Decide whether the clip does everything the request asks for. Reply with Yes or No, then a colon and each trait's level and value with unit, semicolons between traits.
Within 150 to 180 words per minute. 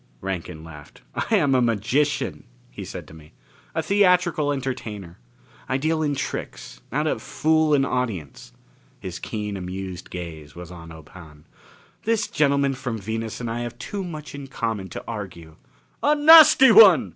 Yes: average, 165 wpm